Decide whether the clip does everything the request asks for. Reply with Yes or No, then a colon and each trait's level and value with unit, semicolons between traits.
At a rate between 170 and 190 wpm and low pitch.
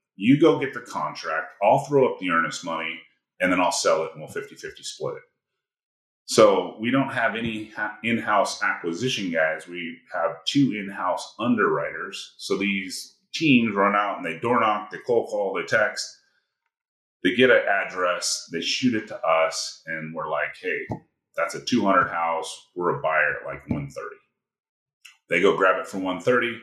Yes: average, 180 wpm; low, 115 Hz